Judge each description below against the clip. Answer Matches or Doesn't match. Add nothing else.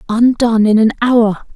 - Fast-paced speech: Doesn't match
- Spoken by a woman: Matches